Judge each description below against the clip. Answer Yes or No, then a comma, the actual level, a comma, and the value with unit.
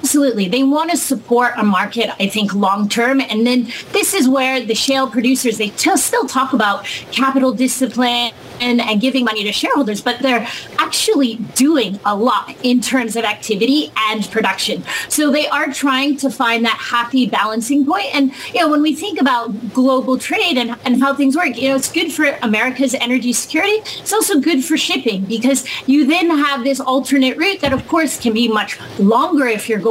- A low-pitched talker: No, very high, 260 Hz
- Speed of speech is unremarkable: Yes, average, 195 wpm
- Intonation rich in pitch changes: No, average, 3.7 semitones